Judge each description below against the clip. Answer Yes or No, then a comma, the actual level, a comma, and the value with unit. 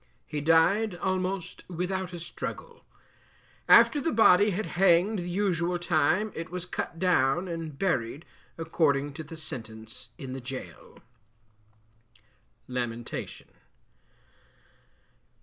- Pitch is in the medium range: Yes, medium, 170 Hz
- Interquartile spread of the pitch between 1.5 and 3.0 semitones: No, average, 4.7 semitones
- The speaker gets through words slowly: Yes, slow, 110 wpm